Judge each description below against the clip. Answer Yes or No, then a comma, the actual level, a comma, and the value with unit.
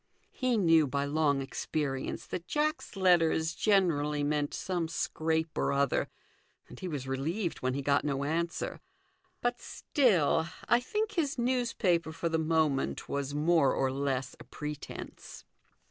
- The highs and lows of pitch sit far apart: No, average, 4.4 semitones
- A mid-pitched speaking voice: Yes, medium, 160 Hz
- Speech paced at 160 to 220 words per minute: No, average, 145 wpm